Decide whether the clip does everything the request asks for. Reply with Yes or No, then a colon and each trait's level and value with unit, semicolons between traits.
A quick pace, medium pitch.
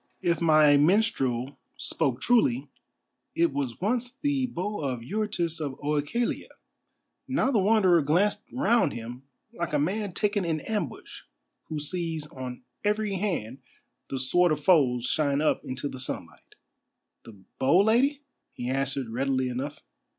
No: average, 140 wpm; medium, 155 Hz